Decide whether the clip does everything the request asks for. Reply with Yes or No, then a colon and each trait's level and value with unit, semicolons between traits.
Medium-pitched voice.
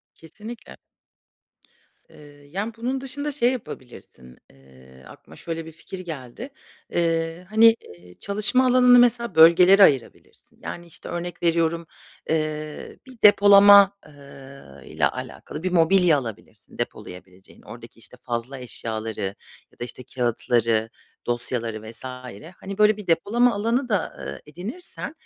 Yes: medium, 165 Hz